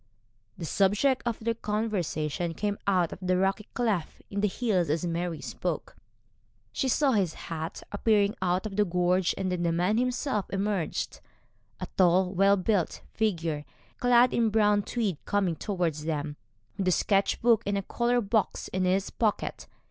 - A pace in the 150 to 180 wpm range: Yes, average, 160 wpm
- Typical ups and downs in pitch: Yes, average, 3.4 semitones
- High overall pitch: Yes, high, 195 Hz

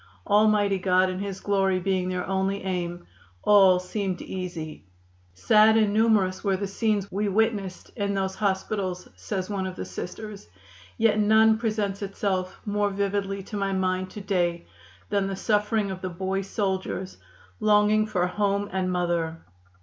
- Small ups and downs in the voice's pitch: Yes, narrow, 2.0 semitones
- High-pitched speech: Yes, high, 195 Hz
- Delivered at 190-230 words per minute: No, average, 155 wpm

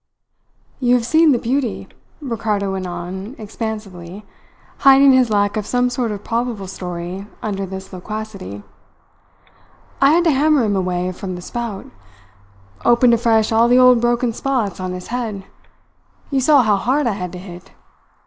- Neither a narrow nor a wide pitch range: Yes, average, 4.4 semitones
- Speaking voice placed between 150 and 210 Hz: No, high, 220 Hz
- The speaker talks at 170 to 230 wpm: No, average, 160 wpm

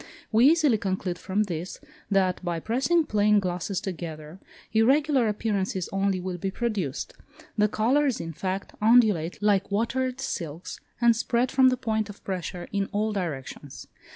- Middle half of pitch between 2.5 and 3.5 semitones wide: No, average, 4.3 semitones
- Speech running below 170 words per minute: Yes, average, 150 wpm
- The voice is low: No, high, 205 Hz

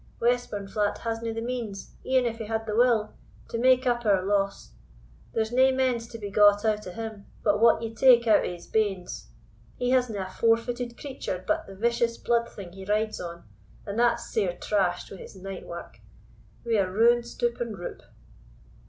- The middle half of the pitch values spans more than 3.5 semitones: No, average, 2.9 semitones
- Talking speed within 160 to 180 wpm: No, average, 190 wpm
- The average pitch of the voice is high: Yes, high, 225 Hz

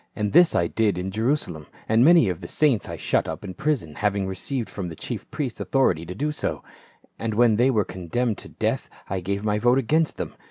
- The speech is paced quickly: Yes, fast, 225 wpm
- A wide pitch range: Yes, wide, 5.8 semitones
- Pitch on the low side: Yes, low, 105 Hz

